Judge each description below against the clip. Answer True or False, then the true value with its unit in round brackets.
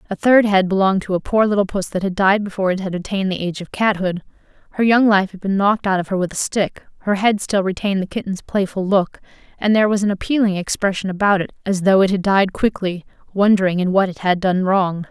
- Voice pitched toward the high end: True (195 Hz)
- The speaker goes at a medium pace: False (240 wpm)